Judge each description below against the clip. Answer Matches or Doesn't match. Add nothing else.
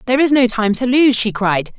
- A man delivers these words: Doesn't match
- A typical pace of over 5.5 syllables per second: Matches